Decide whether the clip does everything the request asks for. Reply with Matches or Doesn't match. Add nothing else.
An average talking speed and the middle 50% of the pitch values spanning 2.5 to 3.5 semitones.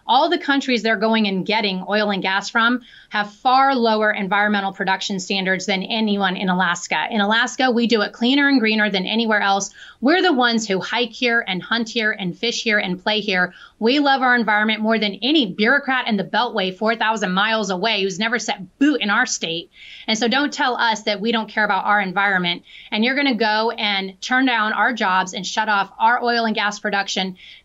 Doesn't match